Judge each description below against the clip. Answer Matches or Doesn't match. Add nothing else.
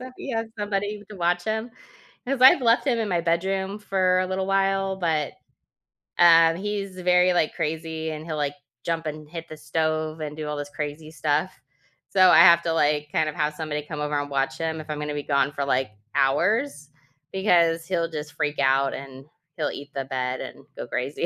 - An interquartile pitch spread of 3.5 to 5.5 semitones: Matches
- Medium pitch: Matches